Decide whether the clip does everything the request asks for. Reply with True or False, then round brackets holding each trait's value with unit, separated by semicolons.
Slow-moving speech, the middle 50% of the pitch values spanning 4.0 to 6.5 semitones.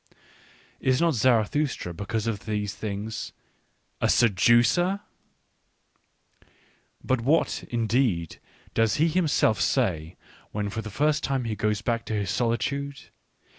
True (125 wpm; 4.7 semitones)